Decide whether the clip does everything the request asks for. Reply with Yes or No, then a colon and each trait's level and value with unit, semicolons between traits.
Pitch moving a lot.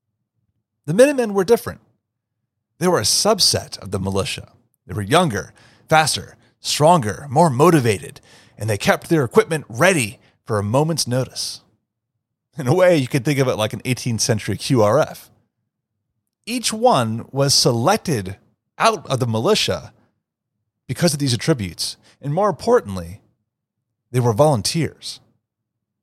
Yes: wide, 6.0 semitones